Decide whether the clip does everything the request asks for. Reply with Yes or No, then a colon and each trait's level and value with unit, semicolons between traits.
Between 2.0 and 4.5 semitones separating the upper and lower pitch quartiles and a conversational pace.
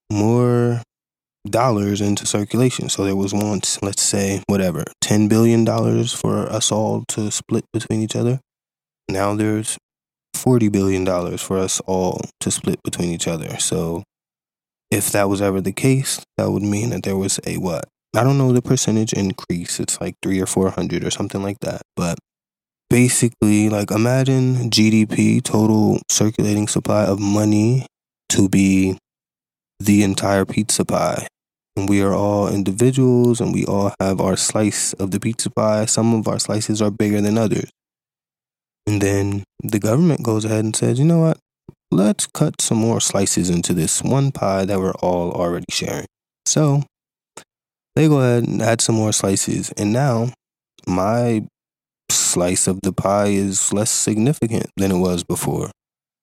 Yes: average, 3.0 semitones; average, 160 wpm